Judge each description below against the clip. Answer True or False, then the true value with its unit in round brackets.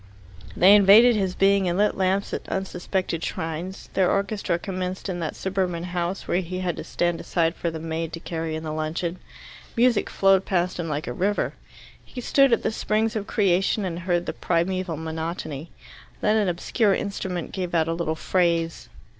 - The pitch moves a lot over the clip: False (2.7 semitones)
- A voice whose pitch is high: False (180 Hz)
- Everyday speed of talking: True (185 wpm)